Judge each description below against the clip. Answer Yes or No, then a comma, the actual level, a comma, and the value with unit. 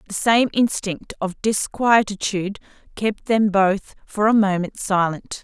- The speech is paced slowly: Yes, slow, 130 wpm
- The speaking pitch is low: No, high, 205 Hz